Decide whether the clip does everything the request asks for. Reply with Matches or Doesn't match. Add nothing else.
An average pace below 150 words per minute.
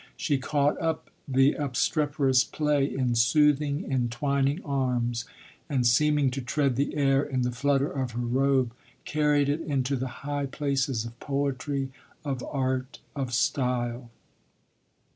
Matches